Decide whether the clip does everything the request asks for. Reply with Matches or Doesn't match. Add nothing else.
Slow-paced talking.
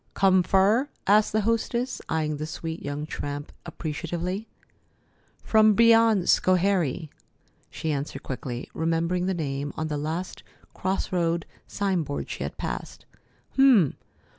Matches